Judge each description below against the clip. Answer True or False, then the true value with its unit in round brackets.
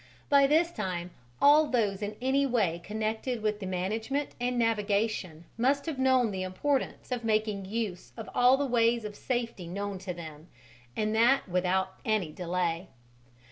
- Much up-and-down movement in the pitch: False (4.9 semitones)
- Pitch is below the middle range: False (215 Hz)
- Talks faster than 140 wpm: True (160 wpm)